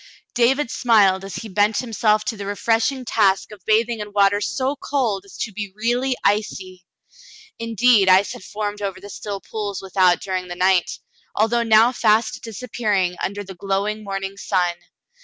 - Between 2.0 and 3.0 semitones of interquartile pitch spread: Yes, average, 2.7 semitones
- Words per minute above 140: Yes, average, 165 wpm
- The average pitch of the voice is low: No, high, 210 Hz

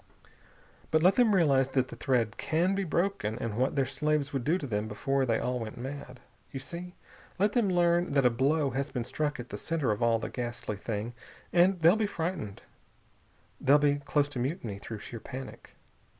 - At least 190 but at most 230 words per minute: Yes, average, 200 wpm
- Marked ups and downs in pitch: Yes, wide, 5.7 semitones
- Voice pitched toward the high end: No, low, 135 Hz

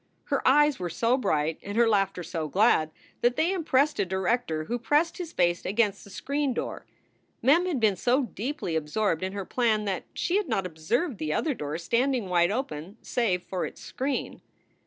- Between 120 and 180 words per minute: No, average, 190 wpm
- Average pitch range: No, wide, 6.9 semitones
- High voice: Yes, high, 220 Hz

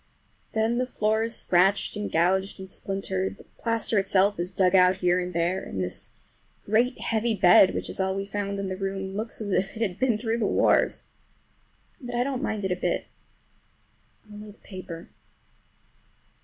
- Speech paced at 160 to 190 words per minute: Yes, average, 180 wpm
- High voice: Yes, high, 195 Hz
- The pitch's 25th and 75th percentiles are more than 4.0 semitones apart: No, average, 2.7 semitones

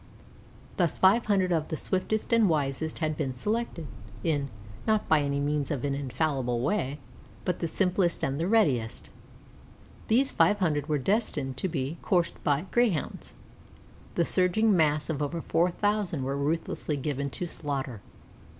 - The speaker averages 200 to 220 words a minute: No, average, 150 wpm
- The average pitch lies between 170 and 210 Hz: No, medium, 160 Hz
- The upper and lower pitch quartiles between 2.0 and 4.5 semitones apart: No, average, 4.9 semitones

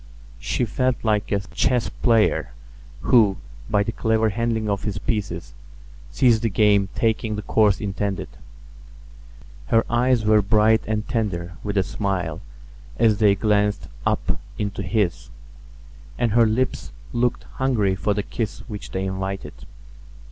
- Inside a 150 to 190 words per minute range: No, average, 140 wpm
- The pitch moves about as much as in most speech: No, narrow, 2.2 semitones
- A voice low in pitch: Yes, low, 105 Hz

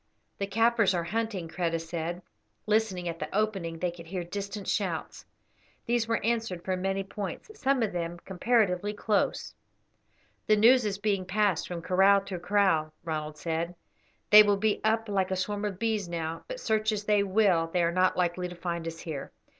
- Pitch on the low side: No, high, 190 Hz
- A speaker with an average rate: Yes, average, 185 wpm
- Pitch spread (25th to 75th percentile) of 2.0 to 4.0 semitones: Yes, average, 3.7 semitones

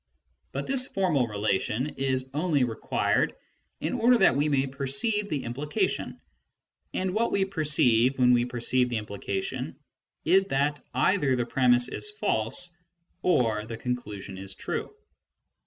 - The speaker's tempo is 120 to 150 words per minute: Yes, average, 140 wpm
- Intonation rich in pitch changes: Yes, wide, 6.2 semitones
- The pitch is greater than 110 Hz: Yes, low, 135 Hz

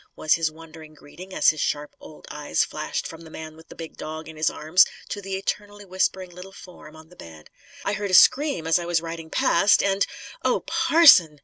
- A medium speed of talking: No, fast, 220 wpm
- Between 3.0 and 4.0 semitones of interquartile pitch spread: Yes, average, 3.5 semitones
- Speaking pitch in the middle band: Yes, medium, 165 Hz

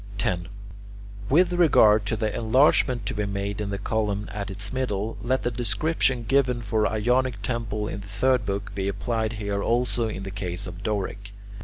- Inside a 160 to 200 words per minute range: Yes, average, 180 wpm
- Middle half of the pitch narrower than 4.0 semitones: Yes, average, 3.3 semitones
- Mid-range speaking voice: No, low, 105 Hz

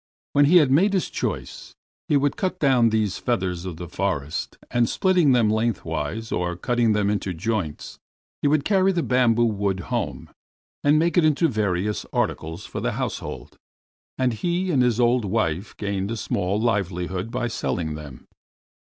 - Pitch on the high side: No, low, 115 Hz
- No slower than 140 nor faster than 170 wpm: Yes, average, 165 wpm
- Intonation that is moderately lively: No, wide, 6.7 semitones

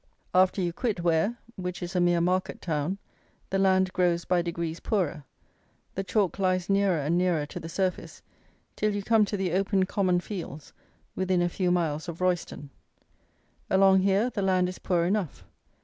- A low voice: No, medium, 185 Hz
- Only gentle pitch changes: Yes, narrow, 2.0 semitones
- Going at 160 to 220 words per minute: Yes, average, 175 wpm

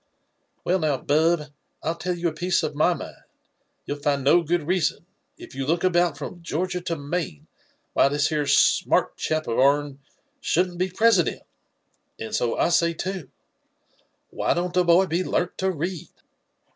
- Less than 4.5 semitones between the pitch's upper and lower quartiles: Yes, average, 3.5 semitones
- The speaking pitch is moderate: Yes, medium, 170 Hz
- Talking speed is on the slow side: No, average, 175 wpm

